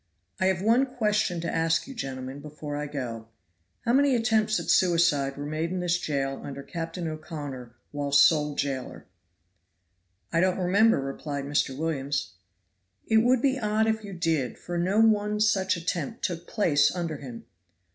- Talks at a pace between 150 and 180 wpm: Yes, average, 165 wpm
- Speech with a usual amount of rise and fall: No, wide, 6.6 semitones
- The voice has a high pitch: No, medium, 165 Hz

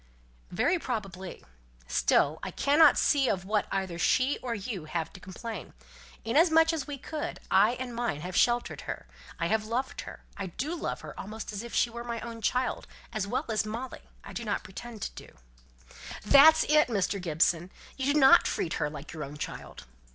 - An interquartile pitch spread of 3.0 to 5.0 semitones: No, wide, 5.6 semitones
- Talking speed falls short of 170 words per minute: No, average, 190 wpm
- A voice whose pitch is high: Yes, high, 225 Hz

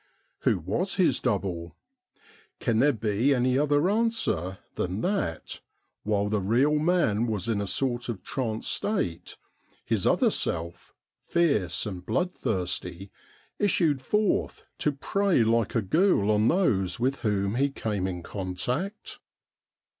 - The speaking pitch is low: Yes, low, 115 Hz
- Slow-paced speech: Yes, slow, 130 wpm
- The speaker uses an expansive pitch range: Yes, wide, 7.2 semitones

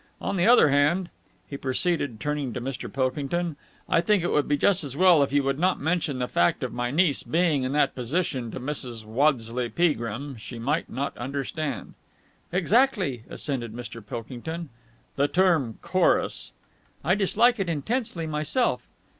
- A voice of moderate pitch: Yes, medium, 145 Hz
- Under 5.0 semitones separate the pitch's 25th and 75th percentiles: No, wide, 5.4 semitones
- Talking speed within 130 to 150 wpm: No, average, 165 wpm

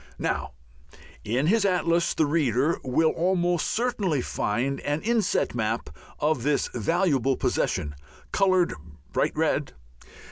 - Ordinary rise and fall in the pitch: No, wide, 5.8 semitones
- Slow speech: Yes, slow, 115 wpm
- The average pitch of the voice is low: No, medium, 155 Hz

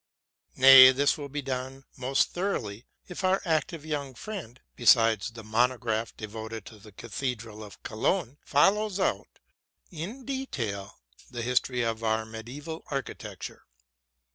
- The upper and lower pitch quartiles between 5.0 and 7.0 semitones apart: Yes, average, 5.3 semitones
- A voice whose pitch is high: No, low, 130 Hz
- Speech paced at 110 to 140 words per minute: Yes, slow, 135 wpm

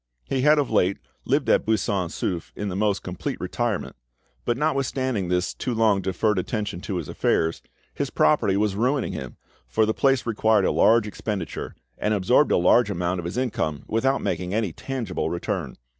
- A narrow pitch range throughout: No, average, 4.6 semitones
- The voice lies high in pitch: No, low, 105 Hz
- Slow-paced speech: No, average, 180 wpm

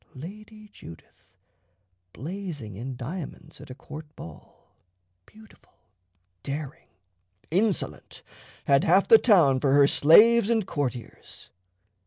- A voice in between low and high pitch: Yes, medium, 155 Hz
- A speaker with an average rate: No, slow, 105 wpm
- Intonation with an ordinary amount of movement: No, wide, 7.0 semitones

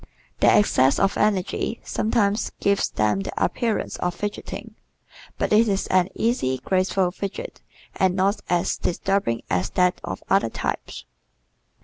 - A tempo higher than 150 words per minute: No, slow, 135 wpm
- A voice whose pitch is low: No, high, 190 Hz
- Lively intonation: No, average, 2.7 semitones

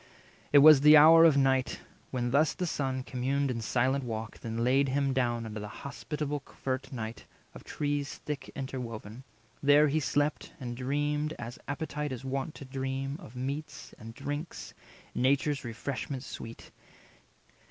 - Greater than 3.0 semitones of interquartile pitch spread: No, narrow, 2.6 semitones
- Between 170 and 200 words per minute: No, average, 155 wpm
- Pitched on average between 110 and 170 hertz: Yes, low, 135 Hz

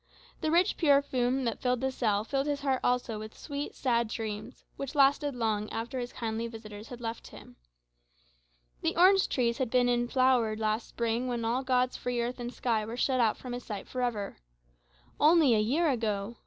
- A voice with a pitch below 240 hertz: No, high, 245 Hz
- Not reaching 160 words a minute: No, average, 195 wpm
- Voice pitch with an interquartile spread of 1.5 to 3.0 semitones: Yes, average, 2.7 semitones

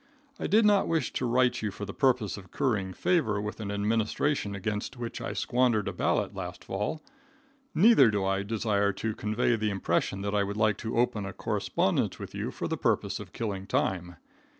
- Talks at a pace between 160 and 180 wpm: No, average, 195 wpm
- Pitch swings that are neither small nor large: Yes, average, 3.4 semitones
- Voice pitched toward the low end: Yes, low, 105 Hz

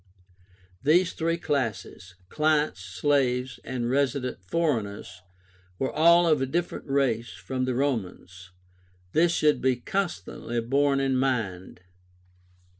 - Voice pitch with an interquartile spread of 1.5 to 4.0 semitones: No, average, 4.8 semitones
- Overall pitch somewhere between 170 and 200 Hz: No, low, 130 Hz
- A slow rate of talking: Yes, slow, 115 wpm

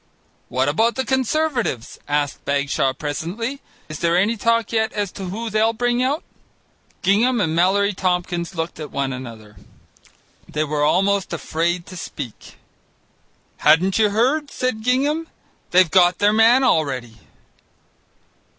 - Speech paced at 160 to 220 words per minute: No, slow, 135 wpm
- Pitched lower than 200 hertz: Yes, high, 190 Hz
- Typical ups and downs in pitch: No, wide, 7.0 semitones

